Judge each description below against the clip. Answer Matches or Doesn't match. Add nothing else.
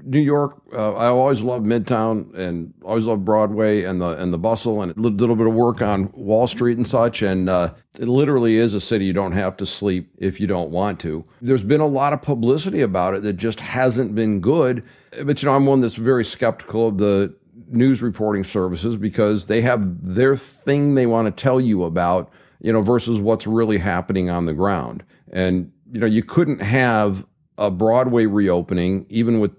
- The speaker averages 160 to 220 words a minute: Matches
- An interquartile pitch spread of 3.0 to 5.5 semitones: Matches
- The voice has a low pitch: Matches